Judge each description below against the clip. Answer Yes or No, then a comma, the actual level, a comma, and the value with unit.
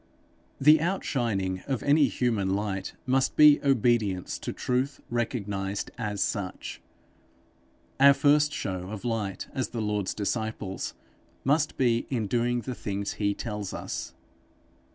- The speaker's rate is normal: No, slow, 130 wpm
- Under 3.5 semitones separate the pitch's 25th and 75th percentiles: No, average, 4.7 semitones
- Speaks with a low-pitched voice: Yes, low, 115 Hz